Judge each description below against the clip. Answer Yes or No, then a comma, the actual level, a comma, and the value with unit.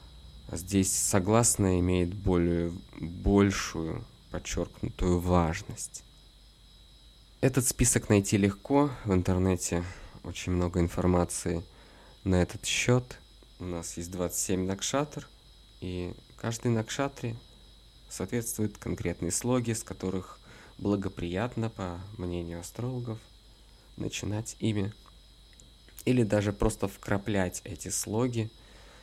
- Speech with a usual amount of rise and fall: Yes, average, 4.2 semitones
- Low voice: Yes, low, 100 Hz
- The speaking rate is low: Yes, slow, 90 wpm